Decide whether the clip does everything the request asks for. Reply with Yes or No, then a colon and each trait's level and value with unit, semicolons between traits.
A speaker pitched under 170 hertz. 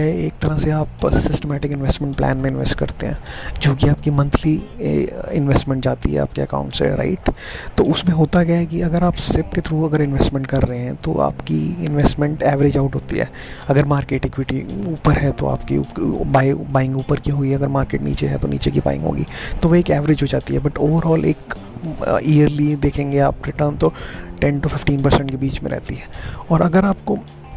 Yes: medium, 140 Hz